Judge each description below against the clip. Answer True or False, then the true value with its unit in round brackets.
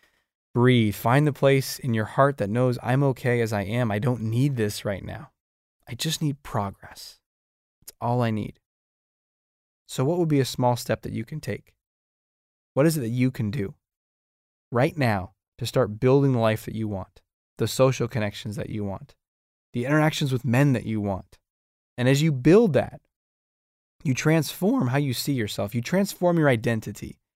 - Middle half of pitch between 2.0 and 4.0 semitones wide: False (4.7 semitones)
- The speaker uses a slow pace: False (185 wpm)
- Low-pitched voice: True (120 Hz)